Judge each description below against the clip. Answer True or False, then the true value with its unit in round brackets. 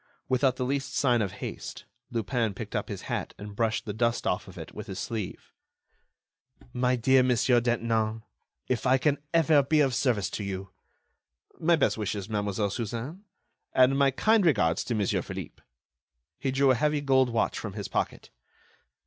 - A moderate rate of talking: True (175 wpm)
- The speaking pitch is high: False (125 Hz)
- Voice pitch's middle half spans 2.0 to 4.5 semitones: True (3.8 semitones)